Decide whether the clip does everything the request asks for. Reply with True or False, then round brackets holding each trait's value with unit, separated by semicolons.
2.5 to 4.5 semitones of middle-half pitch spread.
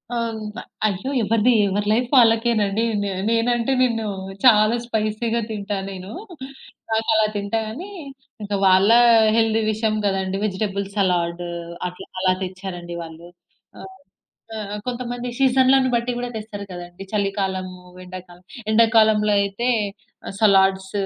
True (3.0 semitones)